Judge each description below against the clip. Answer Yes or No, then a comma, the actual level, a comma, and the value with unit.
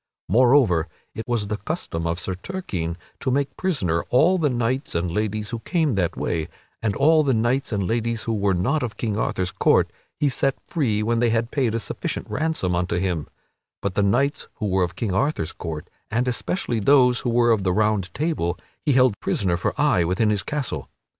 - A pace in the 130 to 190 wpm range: No, average, 200 wpm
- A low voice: Yes, low, 110 Hz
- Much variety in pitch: Yes, wide, 6.0 semitones